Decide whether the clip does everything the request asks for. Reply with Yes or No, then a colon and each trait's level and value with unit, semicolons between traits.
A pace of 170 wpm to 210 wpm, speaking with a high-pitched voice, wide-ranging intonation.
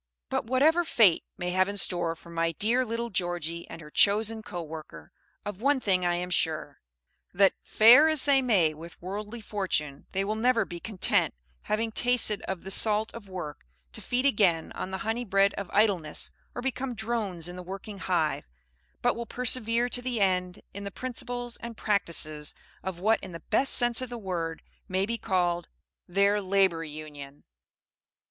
No: average, 180 wpm; high, 200 Hz; average, 4.8 semitones